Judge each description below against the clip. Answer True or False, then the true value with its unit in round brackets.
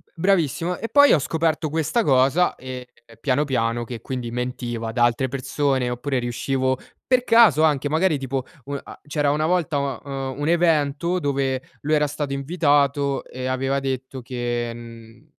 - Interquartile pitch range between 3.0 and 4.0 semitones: True (3.3 semitones)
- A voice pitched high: False (140 Hz)